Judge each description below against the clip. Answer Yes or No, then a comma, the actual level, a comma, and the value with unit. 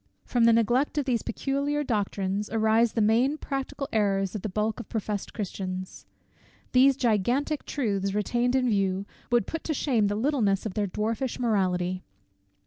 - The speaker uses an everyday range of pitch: Yes, average, 4.3 semitones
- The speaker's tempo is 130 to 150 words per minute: No, average, 160 wpm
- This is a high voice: Yes, high, 220 Hz